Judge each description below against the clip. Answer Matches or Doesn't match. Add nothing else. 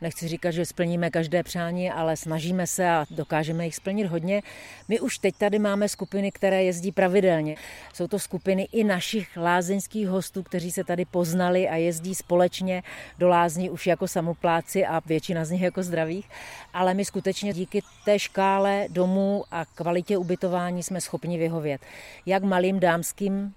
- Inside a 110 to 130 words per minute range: Doesn't match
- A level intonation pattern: Matches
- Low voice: Doesn't match